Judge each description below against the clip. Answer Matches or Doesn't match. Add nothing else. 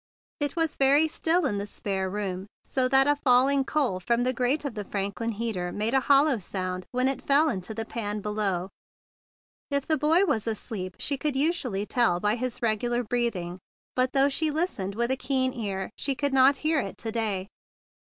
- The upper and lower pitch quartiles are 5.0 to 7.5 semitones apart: Matches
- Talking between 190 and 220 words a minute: Matches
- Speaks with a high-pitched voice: Matches